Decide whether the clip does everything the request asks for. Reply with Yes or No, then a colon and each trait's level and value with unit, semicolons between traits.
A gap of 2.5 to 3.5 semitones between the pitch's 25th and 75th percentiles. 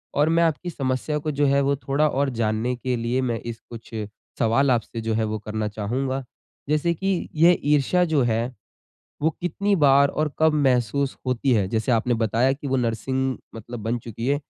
No: average, 3.9 semitones